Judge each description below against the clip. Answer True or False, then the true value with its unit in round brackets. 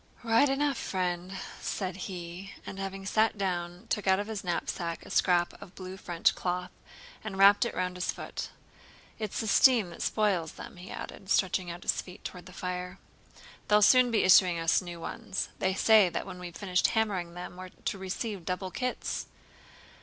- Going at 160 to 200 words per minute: True (185 wpm)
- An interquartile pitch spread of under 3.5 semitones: True (2.4 semitones)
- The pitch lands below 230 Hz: True (185 Hz)